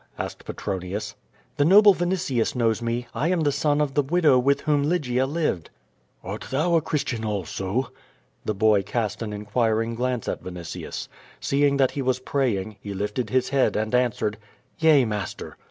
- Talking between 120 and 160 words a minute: No, average, 170 wpm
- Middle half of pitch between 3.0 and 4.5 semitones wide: No, average, 5.3 semitones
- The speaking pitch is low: Yes, low, 125 Hz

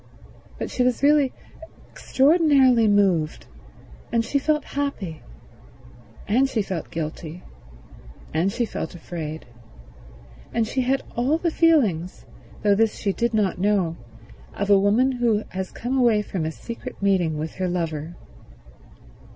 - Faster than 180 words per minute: No, slow, 135 wpm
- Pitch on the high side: Yes, high, 210 Hz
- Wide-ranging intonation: Yes, wide, 6.4 semitones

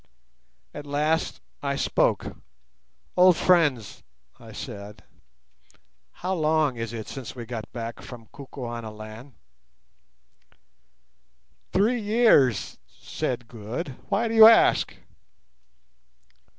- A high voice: No, low, 135 Hz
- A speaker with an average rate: No, slow, 95 wpm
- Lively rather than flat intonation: Yes, wide, 7.4 semitones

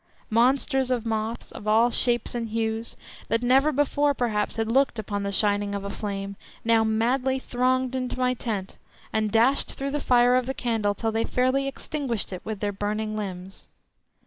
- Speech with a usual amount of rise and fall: Yes, average, 3.2 semitones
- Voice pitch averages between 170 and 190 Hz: No, high, 230 Hz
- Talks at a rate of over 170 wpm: Yes, average, 180 wpm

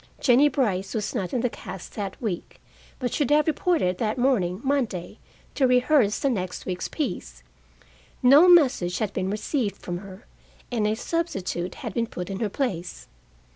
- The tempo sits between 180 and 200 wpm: No, average, 170 wpm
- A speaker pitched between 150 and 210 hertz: No, high, 220 Hz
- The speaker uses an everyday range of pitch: No, wide, 6.2 semitones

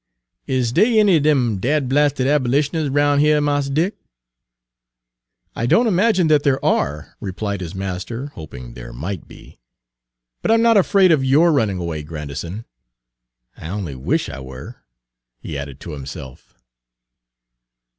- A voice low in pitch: Yes, low, 130 Hz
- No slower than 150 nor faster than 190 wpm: No, average, 140 wpm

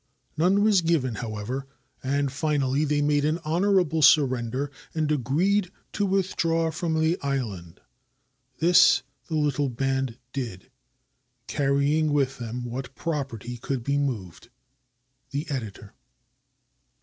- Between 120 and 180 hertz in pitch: Yes, medium, 140 Hz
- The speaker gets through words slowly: Yes, slow, 115 wpm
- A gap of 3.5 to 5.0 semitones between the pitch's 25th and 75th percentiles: Yes, average, 4.0 semitones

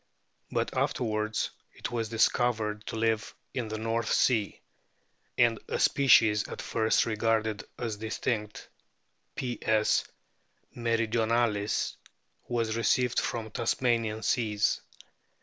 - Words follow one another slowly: Yes, slow, 100 wpm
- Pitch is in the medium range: No, low, 115 Hz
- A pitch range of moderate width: No, narrow, 1.4 semitones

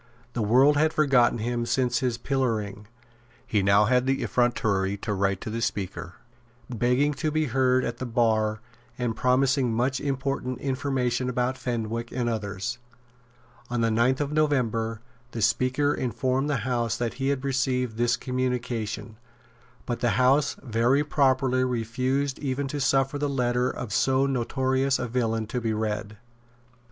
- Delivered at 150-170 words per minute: Yes, average, 155 wpm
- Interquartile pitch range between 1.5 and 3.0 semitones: Yes, average, 2.7 semitones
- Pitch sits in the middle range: No, low, 125 Hz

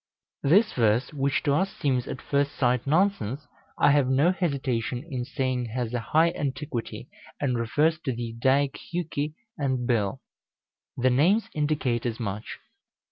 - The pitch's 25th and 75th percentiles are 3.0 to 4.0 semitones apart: Yes, average, 3.7 semitones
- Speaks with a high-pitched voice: No, low, 135 Hz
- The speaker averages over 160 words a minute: No, average, 150 wpm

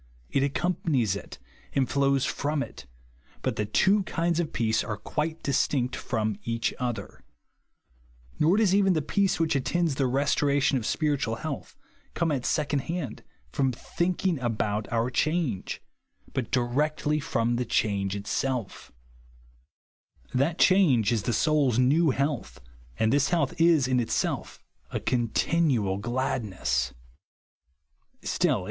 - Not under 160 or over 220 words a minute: No, slow, 135 wpm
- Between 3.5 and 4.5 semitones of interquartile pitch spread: No, average, 5.1 semitones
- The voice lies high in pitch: No, low, 135 Hz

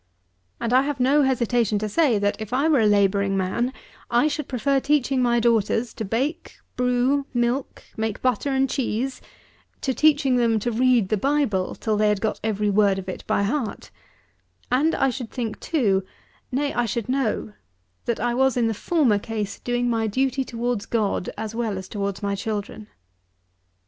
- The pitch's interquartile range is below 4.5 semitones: Yes, average, 4.0 semitones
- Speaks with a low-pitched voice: No, high, 235 Hz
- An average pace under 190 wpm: Yes, average, 180 wpm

